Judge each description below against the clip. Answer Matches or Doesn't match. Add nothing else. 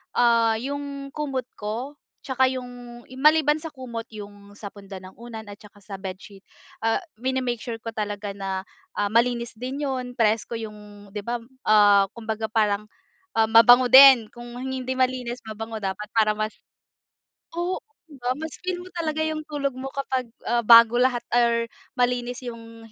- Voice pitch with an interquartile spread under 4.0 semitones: Matches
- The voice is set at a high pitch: Matches